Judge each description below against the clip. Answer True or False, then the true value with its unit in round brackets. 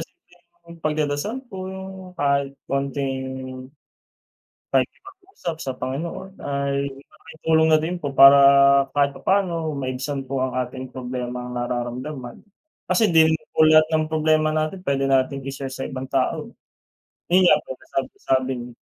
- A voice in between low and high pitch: True (145 Hz)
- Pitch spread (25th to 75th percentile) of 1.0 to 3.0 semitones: False (4.2 semitones)